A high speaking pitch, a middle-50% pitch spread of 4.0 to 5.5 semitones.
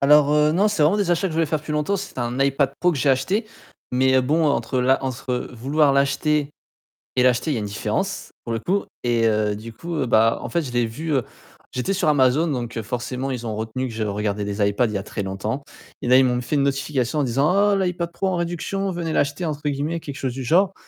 No: low, 135 Hz; average, 4.7 semitones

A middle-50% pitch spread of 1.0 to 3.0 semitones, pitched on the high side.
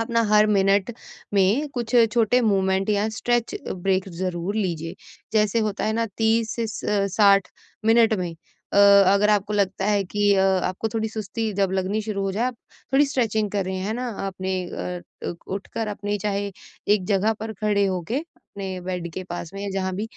Yes: narrow, 2.4 semitones; high, 200 Hz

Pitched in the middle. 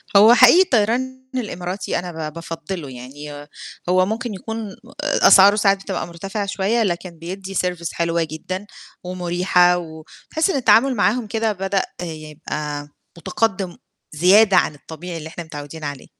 Yes: medium, 180 Hz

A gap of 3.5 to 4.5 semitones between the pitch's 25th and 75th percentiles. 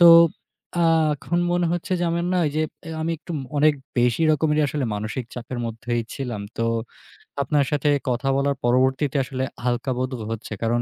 Yes: average, 4.1 semitones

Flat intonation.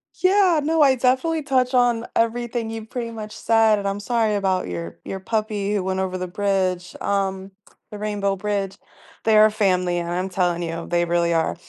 No: average, 3.8 semitones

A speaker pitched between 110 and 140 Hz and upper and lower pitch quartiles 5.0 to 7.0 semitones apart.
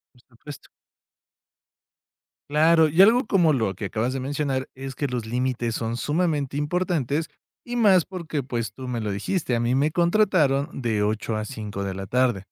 Yes: low, 135 Hz; wide, 5.4 semitones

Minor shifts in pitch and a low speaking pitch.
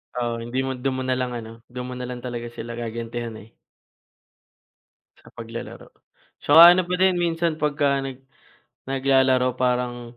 Yes: narrow, 2.3 semitones; low, 125 Hz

